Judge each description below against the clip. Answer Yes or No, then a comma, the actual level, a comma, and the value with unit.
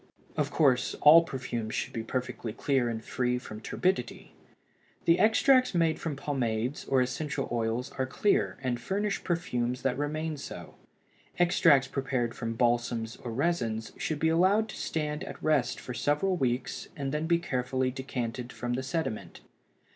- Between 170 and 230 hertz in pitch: No, low, 130 Hz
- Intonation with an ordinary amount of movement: Yes, average, 4.8 semitones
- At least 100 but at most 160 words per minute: Yes, average, 155 wpm